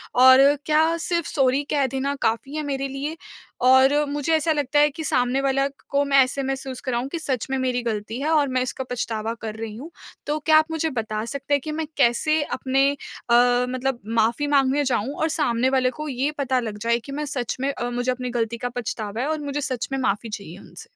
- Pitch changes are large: No, average, 3.1 semitones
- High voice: Yes, very high, 265 Hz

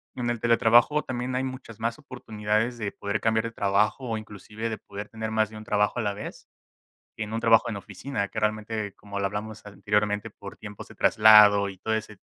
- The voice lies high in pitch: No, low, 110 Hz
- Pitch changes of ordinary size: No, narrow, 1.8 semitones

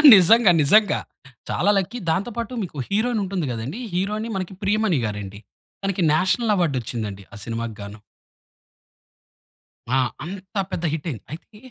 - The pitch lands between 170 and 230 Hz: Yes, medium, 185 Hz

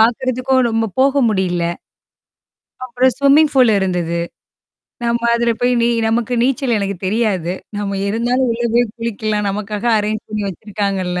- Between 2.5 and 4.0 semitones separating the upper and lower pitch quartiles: Yes, average, 3.6 semitones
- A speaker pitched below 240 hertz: Yes, high, 225 Hz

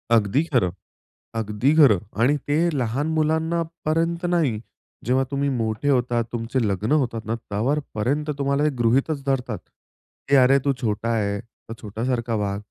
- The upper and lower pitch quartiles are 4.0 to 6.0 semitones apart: Yes, average, 4.6 semitones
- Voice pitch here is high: No, low, 125 Hz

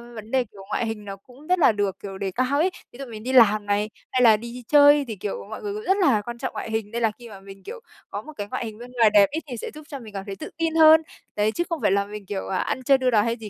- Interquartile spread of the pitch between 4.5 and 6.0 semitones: Yes, average, 4.8 semitones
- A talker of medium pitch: No, high, 230 Hz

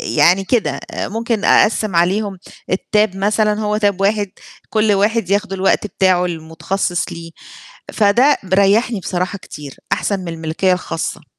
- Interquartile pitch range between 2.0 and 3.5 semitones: Yes, average, 2.9 semitones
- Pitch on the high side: Yes, high, 195 Hz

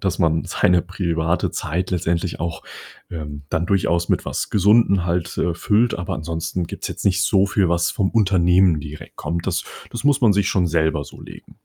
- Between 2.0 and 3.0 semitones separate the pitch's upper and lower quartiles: Yes, average, 2.7 semitones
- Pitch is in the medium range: No, very low, 90 Hz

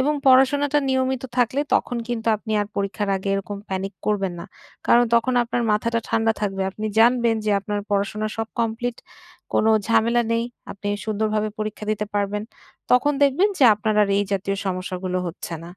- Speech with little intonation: No, average, 3.1 semitones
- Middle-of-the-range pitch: No, high, 215 Hz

